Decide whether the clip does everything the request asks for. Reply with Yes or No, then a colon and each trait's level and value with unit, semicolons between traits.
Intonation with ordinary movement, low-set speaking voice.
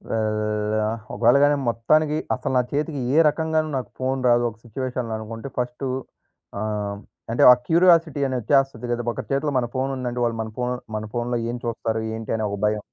Yes: average, 3.5 semitones; low, 120 Hz